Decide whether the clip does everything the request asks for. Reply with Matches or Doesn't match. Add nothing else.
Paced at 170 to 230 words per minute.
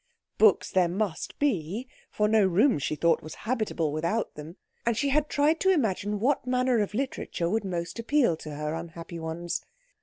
Matches